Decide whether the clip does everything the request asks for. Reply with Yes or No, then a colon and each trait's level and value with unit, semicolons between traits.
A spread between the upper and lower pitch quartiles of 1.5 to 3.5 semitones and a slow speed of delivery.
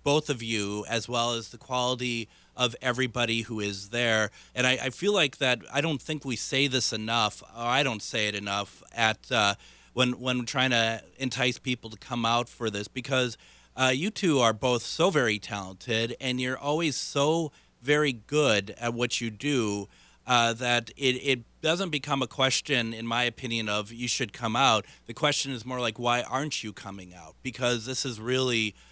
No: narrow, 2.6 semitones; average, 195 wpm